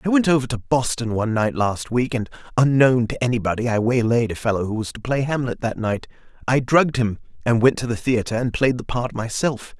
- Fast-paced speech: Yes, fast, 225 wpm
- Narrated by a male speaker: Yes, male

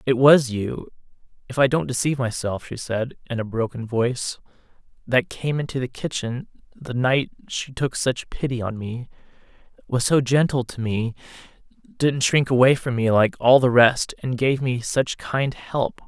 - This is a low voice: Yes, low, 125 Hz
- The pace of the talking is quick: No, average, 175 wpm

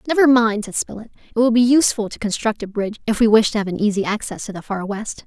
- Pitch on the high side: Yes, high, 220 Hz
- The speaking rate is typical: No, fast, 275 wpm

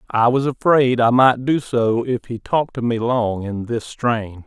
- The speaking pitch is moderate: No, low, 120 Hz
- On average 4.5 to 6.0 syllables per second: No, 4.2 syllables/s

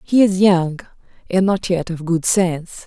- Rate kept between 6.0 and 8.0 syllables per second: No, 4.4 syllables/s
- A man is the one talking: No, female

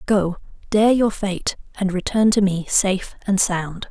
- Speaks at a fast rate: No, average, 170 wpm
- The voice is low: No, high, 195 Hz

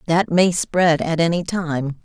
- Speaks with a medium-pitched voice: Yes, medium, 165 Hz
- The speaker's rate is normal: Yes, average, 175 wpm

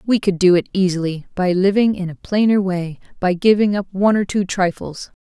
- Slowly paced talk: No, fast, 205 wpm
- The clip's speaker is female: Yes, female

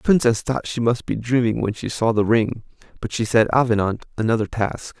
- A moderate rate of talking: No, fast, 215 wpm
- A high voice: No, low, 115 Hz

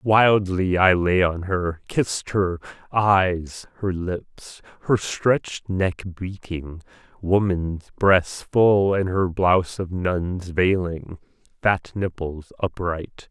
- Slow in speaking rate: Yes, slow, 115 wpm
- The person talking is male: Yes, male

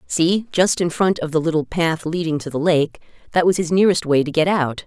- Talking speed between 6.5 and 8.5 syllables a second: No, 5.5 syllables/s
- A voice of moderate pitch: Yes, medium, 165 Hz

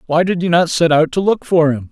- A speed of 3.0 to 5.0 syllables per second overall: No, 5.7 syllables/s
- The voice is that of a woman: No, male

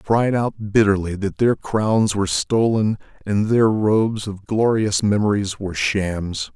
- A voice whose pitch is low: Yes, low, 100 Hz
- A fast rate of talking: No, average, 155 wpm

